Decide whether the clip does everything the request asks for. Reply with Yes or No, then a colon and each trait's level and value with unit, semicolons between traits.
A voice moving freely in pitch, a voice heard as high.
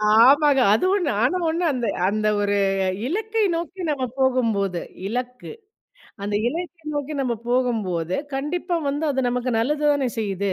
Yes: wide, 5.7 semitones; very high, 260 Hz